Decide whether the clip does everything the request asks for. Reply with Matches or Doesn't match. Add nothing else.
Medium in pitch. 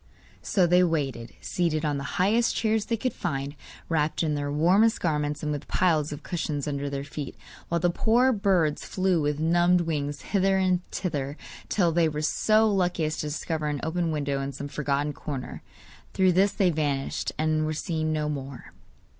Matches